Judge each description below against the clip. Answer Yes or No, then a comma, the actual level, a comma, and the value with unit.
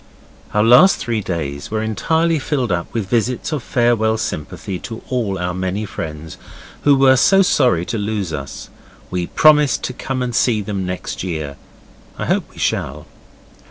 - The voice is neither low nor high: No, low, 110 Hz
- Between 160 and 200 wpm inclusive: Yes, average, 165 wpm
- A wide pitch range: Yes, wide, 5.8 semitones